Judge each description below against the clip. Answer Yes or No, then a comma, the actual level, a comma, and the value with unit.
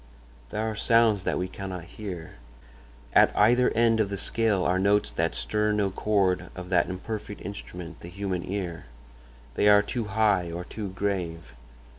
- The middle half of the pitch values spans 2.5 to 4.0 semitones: Yes, average, 2.8 semitones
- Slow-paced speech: No, average, 165 wpm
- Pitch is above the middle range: No, low, 100 Hz